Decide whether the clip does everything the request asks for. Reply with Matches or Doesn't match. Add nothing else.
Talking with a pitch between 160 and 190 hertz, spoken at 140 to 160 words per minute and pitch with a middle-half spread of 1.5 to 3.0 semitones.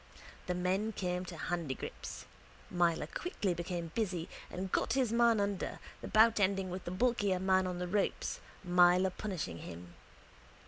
Matches